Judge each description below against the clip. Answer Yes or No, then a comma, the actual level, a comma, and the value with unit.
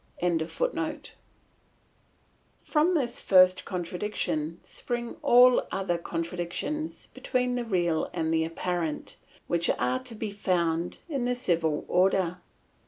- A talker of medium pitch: Yes, medium, 180 Hz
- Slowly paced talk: Yes, slow, 115 wpm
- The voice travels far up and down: Yes, wide, 6.2 semitones